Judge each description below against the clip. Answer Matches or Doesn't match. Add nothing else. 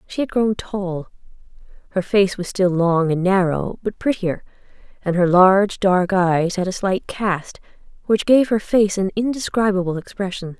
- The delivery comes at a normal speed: Matches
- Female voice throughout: Matches